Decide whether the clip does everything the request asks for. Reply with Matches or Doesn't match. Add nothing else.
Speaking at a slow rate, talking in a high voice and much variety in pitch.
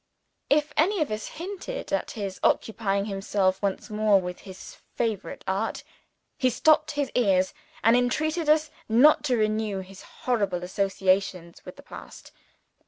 Doesn't match